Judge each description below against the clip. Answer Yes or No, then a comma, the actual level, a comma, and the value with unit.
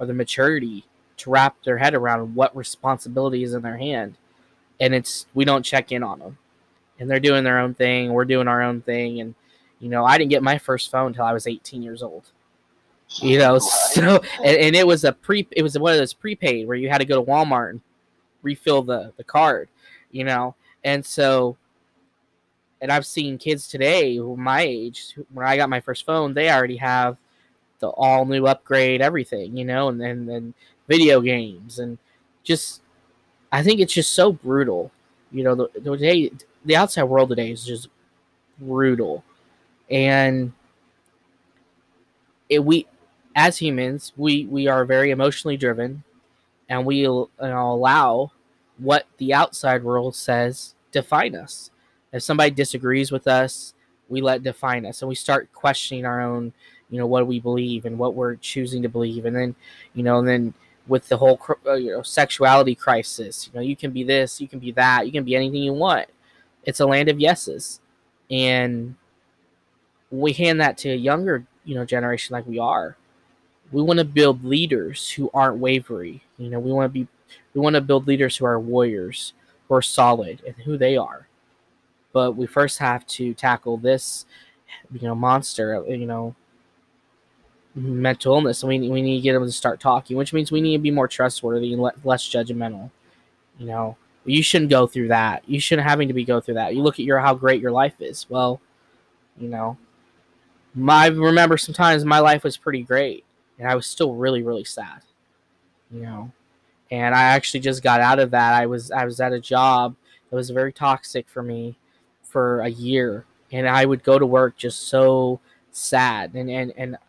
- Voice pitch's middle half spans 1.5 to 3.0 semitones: Yes, narrow, 2.4 semitones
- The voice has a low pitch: Yes, low, 125 Hz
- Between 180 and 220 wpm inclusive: Yes, average, 190 wpm